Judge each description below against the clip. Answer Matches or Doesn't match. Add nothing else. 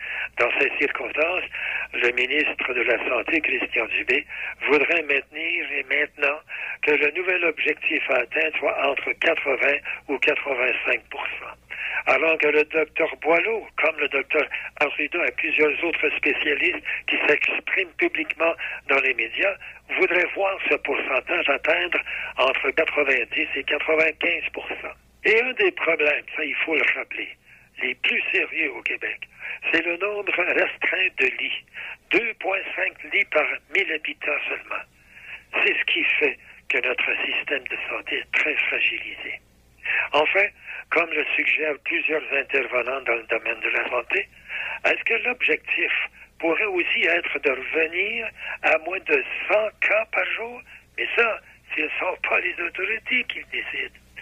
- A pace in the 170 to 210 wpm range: Doesn't match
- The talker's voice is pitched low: Doesn't match